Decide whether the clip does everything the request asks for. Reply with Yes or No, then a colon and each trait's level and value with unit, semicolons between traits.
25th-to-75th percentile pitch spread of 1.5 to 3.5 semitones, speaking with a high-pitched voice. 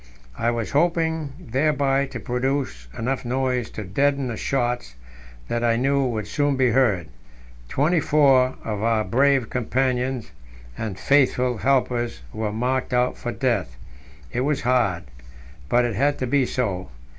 No: average, 3.1 semitones; low, 125 Hz